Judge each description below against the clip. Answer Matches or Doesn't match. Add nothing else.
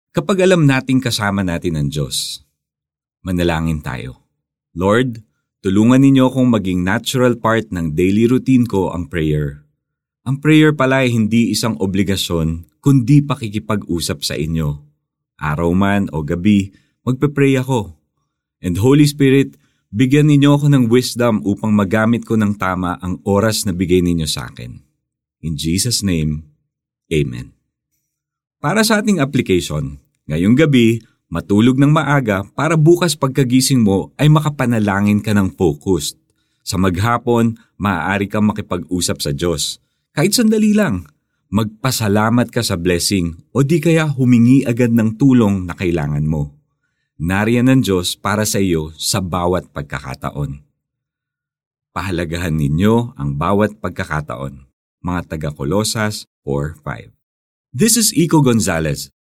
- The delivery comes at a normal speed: Matches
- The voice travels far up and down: Matches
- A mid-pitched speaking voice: Doesn't match